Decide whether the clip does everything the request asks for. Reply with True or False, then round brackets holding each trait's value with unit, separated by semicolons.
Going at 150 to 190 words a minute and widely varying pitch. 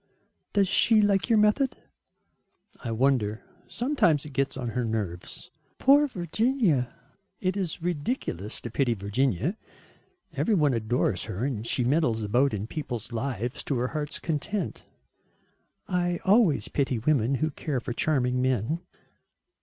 False (140 wpm; 7.1 semitones)